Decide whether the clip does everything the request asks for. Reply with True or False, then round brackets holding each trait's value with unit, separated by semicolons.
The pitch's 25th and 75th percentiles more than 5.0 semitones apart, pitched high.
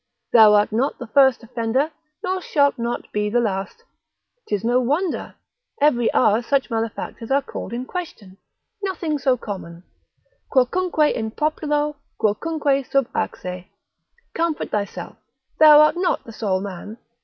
True (5.5 semitones; 250 Hz)